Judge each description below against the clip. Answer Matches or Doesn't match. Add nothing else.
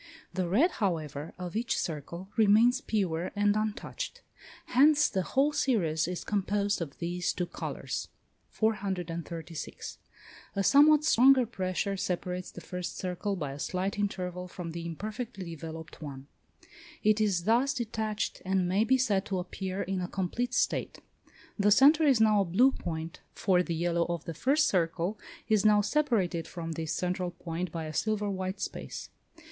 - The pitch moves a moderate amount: Matches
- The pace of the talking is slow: Doesn't match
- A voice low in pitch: Doesn't match